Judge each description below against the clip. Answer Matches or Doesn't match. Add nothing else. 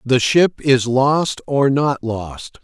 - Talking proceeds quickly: Doesn't match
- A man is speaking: Matches